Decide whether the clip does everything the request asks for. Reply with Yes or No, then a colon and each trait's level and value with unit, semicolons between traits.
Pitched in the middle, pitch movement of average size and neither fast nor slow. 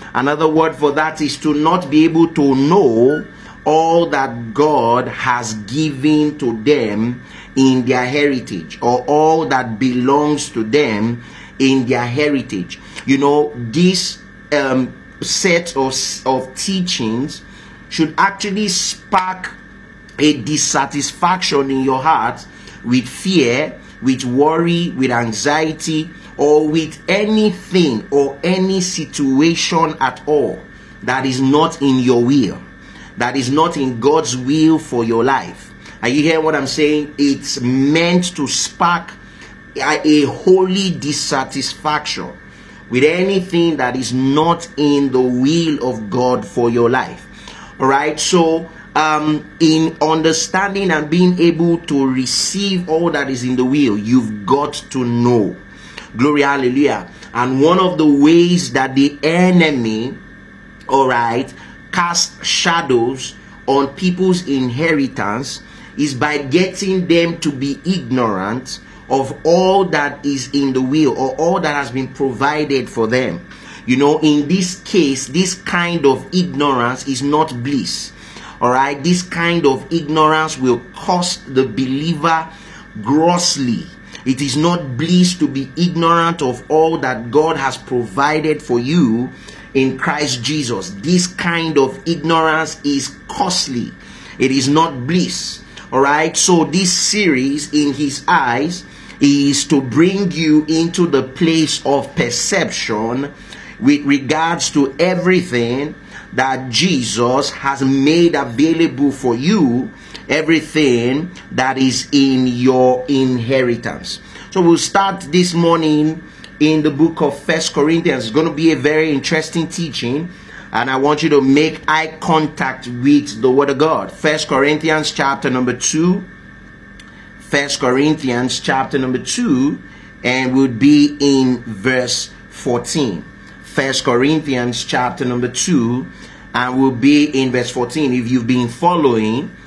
No: medium, 150 Hz; average, 4.0 semitones; slow, 130 wpm